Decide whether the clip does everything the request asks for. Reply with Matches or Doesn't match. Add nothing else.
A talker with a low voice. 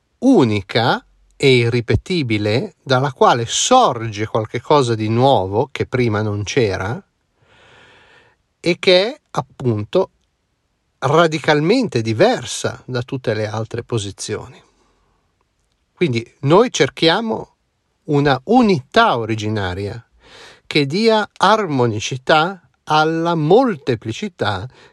Matches